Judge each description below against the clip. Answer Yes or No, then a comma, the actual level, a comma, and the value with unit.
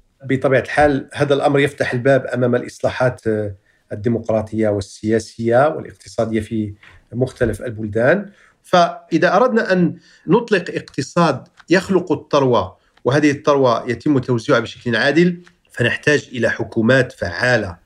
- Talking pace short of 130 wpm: Yes, average, 105 wpm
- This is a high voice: No, low, 130 Hz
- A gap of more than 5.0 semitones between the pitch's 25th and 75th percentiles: Yes, wide, 5.6 semitones